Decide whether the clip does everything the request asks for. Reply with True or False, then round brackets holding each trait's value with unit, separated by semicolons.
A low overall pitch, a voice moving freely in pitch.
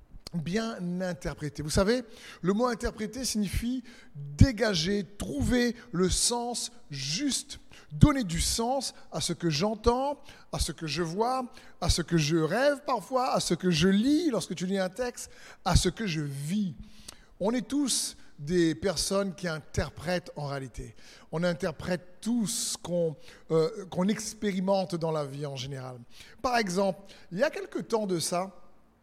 False (190 Hz; 6.0 semitones)